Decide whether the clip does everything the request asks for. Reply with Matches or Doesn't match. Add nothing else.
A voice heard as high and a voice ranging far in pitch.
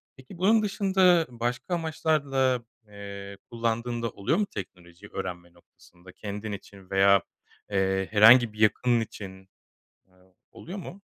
Doesn't match